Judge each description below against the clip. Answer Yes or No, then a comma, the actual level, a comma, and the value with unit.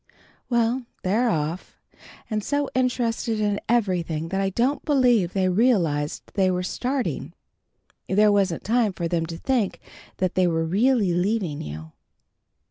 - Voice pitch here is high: Yes, high, 200 Hz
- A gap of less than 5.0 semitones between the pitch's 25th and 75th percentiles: No, wide, 5.5 semitones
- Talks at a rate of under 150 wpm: Yes, average, 140 wpm